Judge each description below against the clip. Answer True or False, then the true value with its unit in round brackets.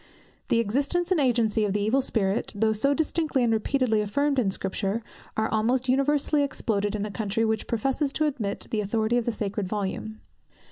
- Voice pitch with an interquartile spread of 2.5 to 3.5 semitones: False (4.5 semitones)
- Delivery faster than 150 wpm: True (185 wpm)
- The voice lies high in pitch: True (225 Hz)